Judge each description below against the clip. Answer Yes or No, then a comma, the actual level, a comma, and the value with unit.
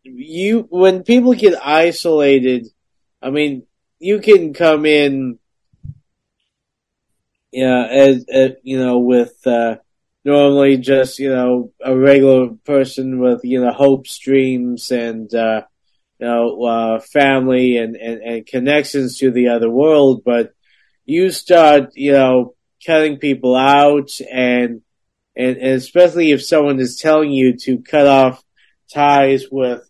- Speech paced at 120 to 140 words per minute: Yes, slow, 135 wpm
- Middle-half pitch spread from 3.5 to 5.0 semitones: No, average, 2.8 semitones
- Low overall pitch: Yes, low, 130 Hz